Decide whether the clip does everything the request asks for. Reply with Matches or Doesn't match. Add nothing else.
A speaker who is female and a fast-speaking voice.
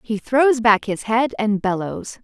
Doesn't match